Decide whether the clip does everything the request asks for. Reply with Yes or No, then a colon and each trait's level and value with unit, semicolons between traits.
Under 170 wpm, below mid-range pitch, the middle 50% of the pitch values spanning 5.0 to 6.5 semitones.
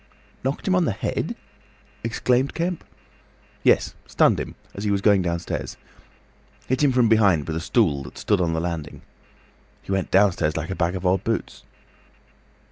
Yes: average, 160 wpm; very low, 95 Hz; wide, 5.6 semitones